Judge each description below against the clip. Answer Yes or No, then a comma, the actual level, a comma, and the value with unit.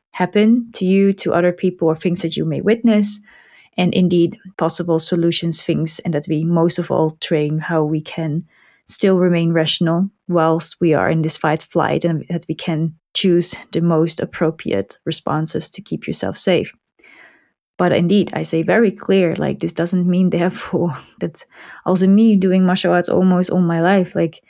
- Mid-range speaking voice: Yes, medium, 170 Hz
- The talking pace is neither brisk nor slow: Yes, average, 175 wpm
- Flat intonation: Yes, narrow, 2.3 semitones